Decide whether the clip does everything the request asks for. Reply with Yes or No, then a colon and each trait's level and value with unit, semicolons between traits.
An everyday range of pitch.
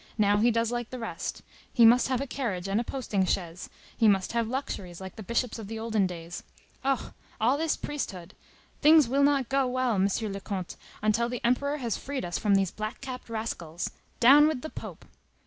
Yes: average, 4.7 semitones